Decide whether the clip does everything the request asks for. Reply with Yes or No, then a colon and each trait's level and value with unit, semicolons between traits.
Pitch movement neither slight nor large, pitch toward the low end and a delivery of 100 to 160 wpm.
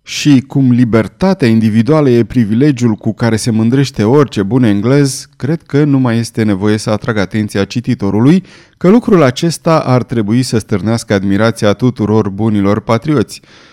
Yes: average, 4.4 semitones; low, 115 Hz; average, 150 wpm